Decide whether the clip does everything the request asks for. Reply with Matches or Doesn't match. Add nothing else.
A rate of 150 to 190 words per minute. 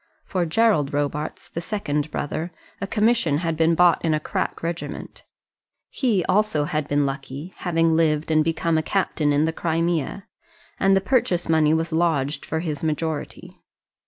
Matches